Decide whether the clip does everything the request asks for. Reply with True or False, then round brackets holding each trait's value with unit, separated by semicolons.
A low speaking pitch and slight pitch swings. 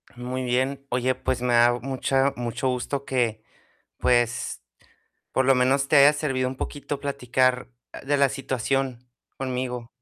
True (130 Hz; 1.7 semitones)